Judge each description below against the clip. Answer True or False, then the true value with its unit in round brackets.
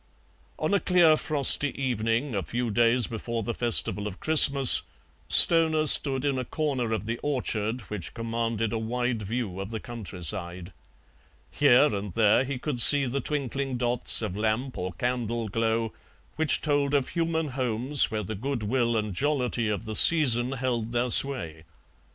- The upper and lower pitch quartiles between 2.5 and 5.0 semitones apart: True (3.9 semitones)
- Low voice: True (120 Hz)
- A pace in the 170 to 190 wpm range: False (160 wpm)